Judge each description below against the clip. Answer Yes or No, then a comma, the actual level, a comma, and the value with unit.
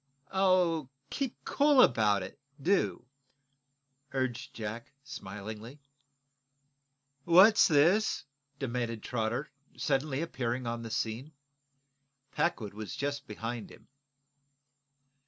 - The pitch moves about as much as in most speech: No, wide, 6.3 semitones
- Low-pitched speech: Yes, low, 130 Hz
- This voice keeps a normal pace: No, slow, 90 wpm